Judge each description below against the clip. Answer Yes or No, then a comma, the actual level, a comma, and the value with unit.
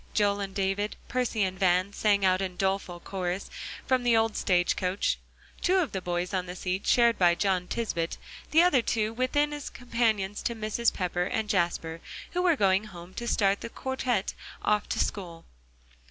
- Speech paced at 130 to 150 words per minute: No, average, 185 wpm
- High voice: Yes, high, 200 Hz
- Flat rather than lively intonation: No, average, 4.2 semitones